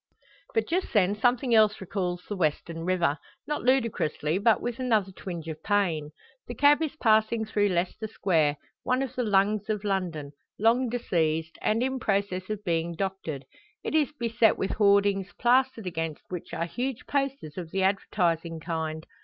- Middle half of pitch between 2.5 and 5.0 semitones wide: No, wide, 5.5 semitones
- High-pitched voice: Yes, high, 200 Hz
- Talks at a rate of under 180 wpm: Yes, average, 165 wpm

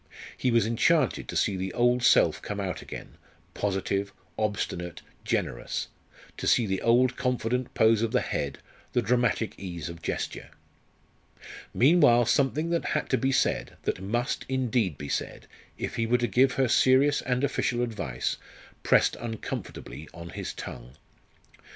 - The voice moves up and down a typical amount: Yes, average, 4.6 semitones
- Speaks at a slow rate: No, average, 150 wpm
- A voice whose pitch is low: Yes, low, 115 Hz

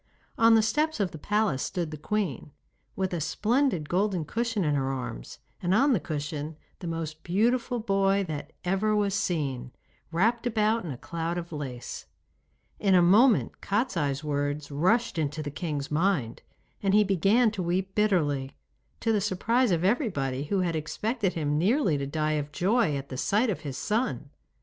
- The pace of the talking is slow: No, average, 175 wpm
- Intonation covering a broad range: Yes, wide, 6.1 semitones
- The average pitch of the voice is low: No, medium, 180 Hz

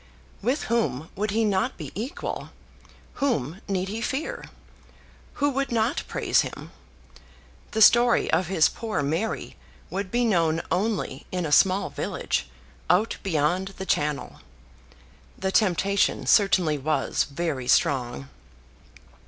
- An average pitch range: No, wide, 5.8 semitones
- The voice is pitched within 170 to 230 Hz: Yes, high, 190 Hz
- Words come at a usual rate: No, slow, 125 wpm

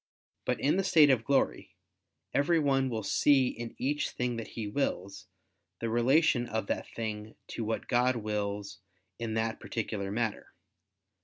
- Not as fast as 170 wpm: Yes, average, 155 wpm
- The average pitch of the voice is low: Yes, low, 115 Hz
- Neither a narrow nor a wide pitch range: Yes, average, 3.6 semitones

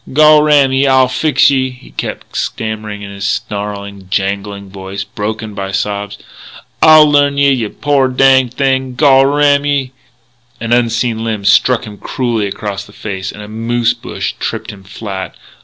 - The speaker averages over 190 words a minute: No, average, 170 wpm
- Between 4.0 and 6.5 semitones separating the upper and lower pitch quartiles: Yes, average, 4.8 semitones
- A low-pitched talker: Yes, low, 115 Hz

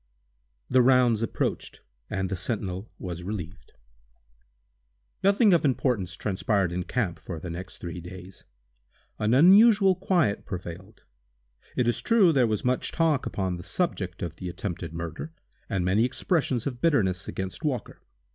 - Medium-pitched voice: No, low, 105 Hz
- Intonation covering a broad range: Yes, wide, 7.0 semitones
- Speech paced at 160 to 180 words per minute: No, average, 145 wpm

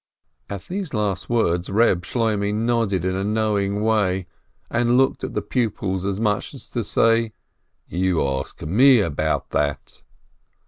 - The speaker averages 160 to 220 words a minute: No, average, 150 wpm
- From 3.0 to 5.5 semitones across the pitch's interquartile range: Yes, average, 3.6 semitones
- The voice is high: No, low, 105 Hz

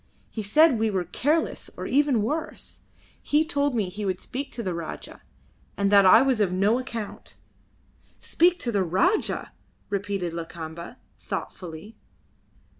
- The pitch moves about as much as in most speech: No, wide, 6.6 semitones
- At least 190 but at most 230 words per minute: No, average, 145 wpm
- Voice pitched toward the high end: Yes, high, 210 Hz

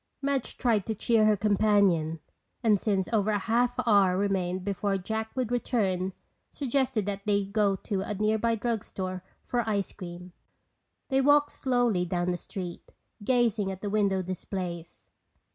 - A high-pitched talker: Yes, high, 205 Hz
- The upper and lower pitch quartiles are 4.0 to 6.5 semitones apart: No, average, 3.4 semitones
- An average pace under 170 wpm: Yes, average, 155 wpm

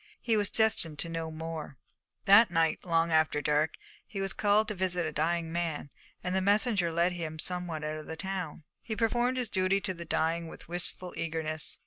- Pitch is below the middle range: No, medium, 170 Hz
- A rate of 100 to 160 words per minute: No, average, 195 wpm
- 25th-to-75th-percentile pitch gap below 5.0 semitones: Yes, average, 3.3 semitones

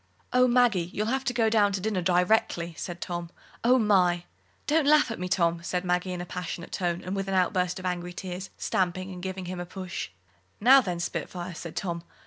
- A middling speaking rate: No, fast, 210 wpm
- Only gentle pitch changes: No, average, 3.1 semitones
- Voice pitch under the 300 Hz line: Yes, medium, 185 Hz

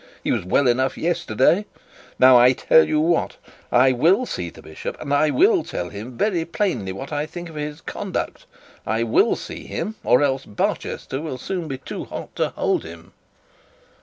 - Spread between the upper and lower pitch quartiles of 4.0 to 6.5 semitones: Yes, wide, 5.5 semitones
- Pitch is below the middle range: No, medium, 145 Hz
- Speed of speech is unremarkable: Yes, average, 190 wpm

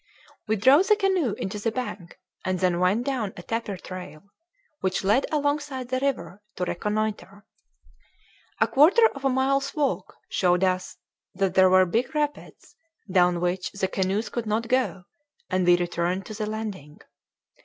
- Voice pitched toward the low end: No, high, 210 Hz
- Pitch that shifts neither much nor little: No, wide, 6.0 semitones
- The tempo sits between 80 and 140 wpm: No, average, 160 wpm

